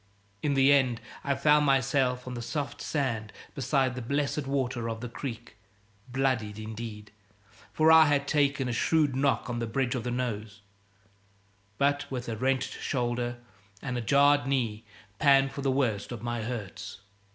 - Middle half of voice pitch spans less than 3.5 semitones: Yes, average, 3.0 semitones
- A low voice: Yes, low, 130 Hz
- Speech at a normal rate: Yes, average, 165 wpm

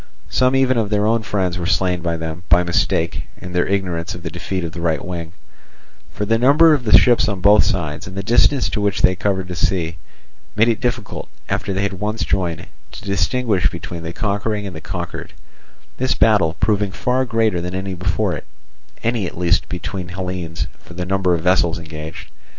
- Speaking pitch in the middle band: No, very low, 95 Hz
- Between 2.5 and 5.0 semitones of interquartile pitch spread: Yes, average, 3.5 semitones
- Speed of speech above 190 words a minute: Yes, average, 200 wpm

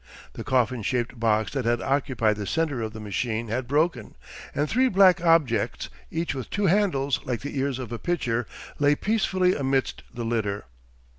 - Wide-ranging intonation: Yes, wide, 5.9 semitones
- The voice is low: Yes, low, 130 Hz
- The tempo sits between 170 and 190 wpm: Yes, average, 175 wpm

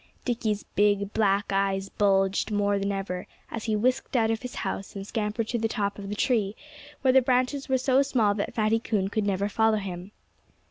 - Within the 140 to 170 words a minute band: No, average, 200 wpm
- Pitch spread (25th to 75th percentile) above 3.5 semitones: No, narrow, 2.5 semitones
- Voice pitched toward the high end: Yes, high, 210 Hz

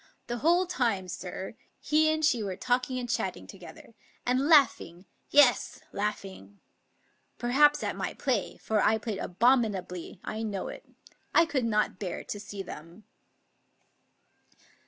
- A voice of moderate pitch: No, high, 225 Hz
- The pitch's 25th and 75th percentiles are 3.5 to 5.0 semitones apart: No, wide, 5.4 semitones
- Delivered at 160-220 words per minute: No, average, 140 wpm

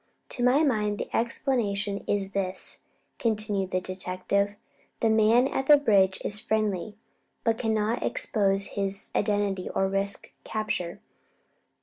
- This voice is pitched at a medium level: No, high, 205 Hz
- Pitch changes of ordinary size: No, narrow, 2.3 semitones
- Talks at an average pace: No, slow, 125 wpm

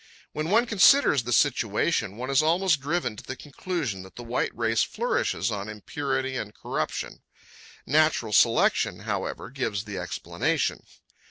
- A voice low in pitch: Yes, low, 130 Hz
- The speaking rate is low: No, average, 145 wpm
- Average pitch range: No, wide, 6.2 semitones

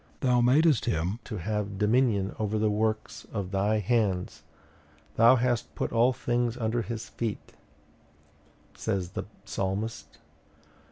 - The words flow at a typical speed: No, slow, 125 wpm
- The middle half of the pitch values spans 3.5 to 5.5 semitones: No, average, 3.0 semitones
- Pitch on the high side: No, low, 110 Hz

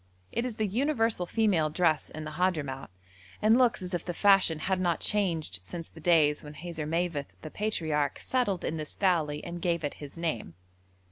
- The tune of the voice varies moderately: Yes, average, 4.2 semitones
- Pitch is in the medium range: Yes, medium, 170 Hz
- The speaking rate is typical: Yes, average, 185 wpm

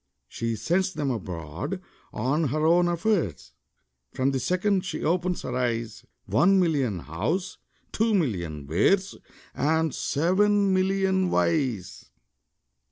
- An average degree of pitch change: No, wide, 8.3 semitones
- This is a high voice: No, medium, 160 Hz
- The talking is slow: Yes, slow, 115 wpm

